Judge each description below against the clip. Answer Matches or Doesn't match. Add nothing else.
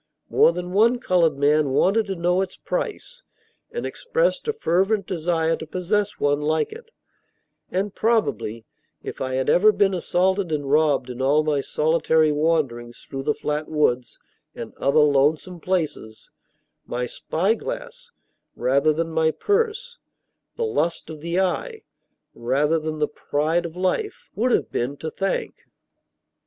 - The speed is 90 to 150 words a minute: Matches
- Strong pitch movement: Doesn't match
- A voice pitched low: Doesn't match